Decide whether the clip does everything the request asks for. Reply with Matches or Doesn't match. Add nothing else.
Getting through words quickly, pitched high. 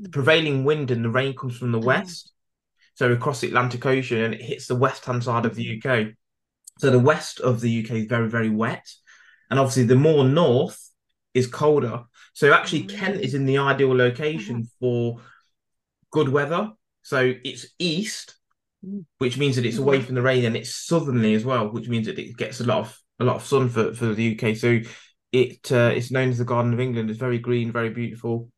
Doesn't match